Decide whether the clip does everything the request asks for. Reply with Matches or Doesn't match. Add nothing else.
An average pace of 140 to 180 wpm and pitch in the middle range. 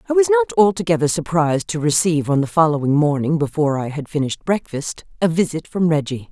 Doesn't match